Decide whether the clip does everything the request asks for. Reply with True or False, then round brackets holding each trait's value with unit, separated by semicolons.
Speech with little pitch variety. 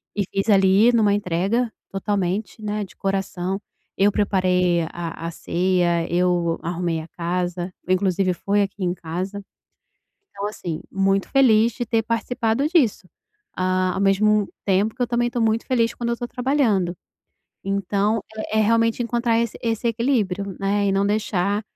False (3.6 semitones)